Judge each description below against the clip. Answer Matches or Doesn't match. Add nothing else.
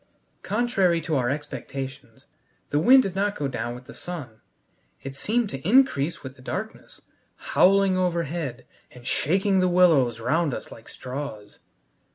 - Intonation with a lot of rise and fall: Matches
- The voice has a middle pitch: Matches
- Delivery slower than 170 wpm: Matches